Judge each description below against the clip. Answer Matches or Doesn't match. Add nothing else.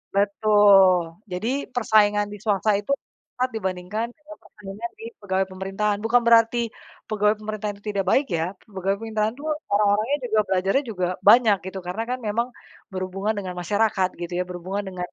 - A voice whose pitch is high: Matches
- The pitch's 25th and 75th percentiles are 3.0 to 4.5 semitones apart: Doesn't match